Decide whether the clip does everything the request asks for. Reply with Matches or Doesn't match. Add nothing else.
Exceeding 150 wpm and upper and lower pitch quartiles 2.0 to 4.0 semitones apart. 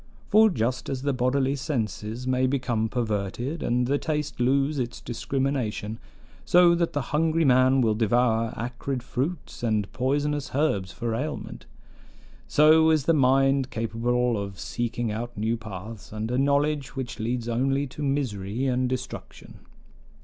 Doesn't match